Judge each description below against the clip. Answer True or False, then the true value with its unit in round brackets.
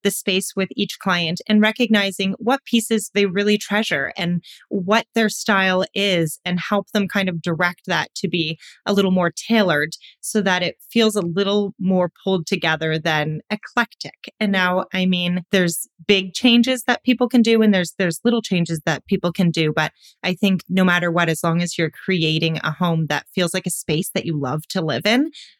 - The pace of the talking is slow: False (200 wpm)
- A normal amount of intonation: True (3.4 semitones)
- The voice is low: False (190 Hz)